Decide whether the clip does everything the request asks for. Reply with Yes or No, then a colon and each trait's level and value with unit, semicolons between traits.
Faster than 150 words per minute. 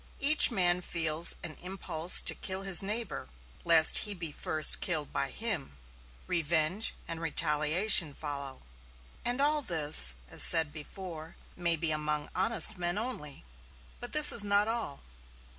No: average, 140 wpm